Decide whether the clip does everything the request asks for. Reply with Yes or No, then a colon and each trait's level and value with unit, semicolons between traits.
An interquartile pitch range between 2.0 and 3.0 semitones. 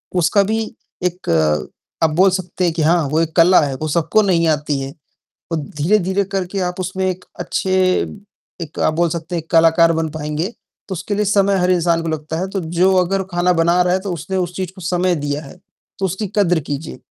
Yes: average, 2.7 semitones